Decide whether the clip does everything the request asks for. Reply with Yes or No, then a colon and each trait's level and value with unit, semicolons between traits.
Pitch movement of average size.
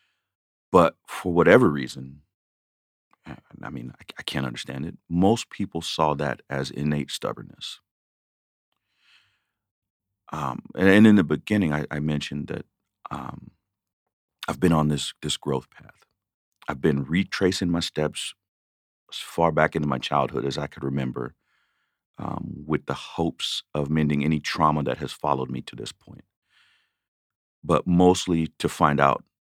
Yes: average, 3.7 semitones